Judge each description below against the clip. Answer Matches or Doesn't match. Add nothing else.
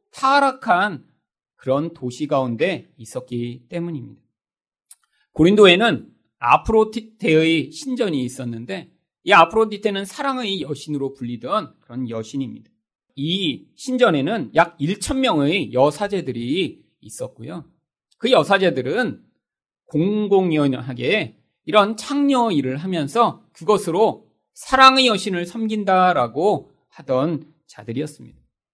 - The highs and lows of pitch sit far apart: Matches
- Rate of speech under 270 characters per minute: Matches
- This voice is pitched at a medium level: Matches